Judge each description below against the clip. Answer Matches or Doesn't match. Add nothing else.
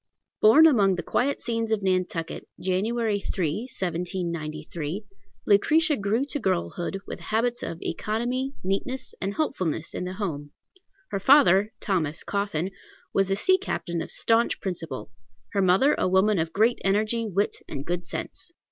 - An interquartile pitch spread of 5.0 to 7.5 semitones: Doesn't match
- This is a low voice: Doesn't match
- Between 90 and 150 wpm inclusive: Matches